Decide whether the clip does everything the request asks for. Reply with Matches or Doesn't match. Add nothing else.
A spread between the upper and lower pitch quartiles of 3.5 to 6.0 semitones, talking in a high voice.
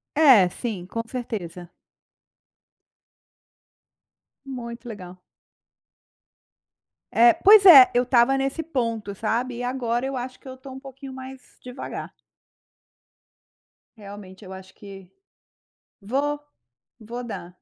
Matches